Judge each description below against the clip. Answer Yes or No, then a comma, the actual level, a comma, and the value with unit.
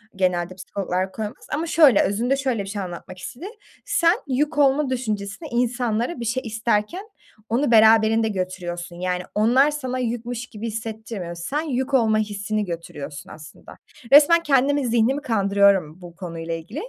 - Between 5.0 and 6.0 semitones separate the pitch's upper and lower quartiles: Yes, wide, 5.5 semitones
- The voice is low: No, high, 220 Hz